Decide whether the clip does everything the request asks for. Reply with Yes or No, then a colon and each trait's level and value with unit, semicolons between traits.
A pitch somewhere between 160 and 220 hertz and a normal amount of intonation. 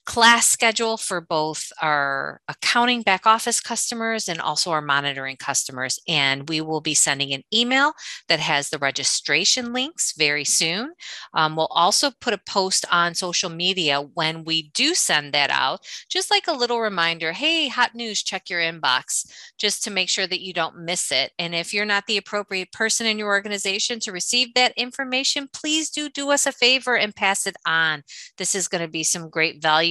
No: high, 190 Hz; wide, 6.7 semitones